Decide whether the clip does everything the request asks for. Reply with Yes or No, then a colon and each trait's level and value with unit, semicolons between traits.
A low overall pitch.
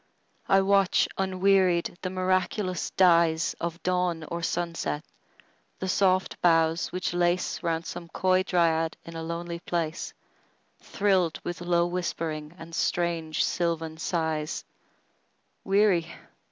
No: medium, 175 Hz